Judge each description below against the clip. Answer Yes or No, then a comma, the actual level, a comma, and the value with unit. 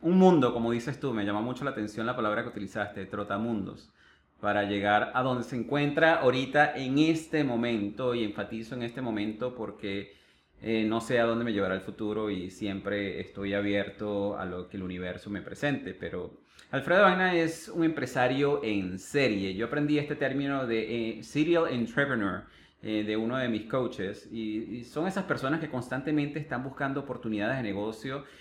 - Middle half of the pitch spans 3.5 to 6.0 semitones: Yes, average, 5.1 semitones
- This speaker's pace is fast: No, average, 180 wpm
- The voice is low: Yes, low, 115 Hz